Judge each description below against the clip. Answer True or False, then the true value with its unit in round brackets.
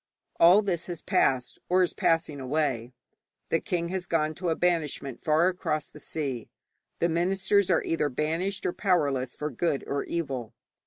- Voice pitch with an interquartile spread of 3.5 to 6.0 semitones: True (3.8 semitones)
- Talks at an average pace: True (165 wpm)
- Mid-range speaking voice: True (165 Hz)